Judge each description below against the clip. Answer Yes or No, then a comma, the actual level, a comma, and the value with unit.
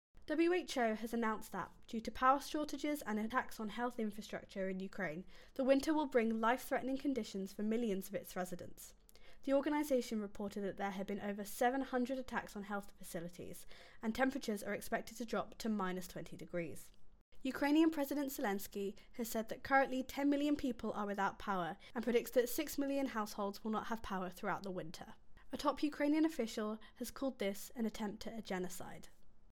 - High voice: Yes, high, 225 Hz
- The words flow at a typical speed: Yes, average, 175 wpm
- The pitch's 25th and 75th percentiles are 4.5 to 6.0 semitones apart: Yes, average, 4.9 semitones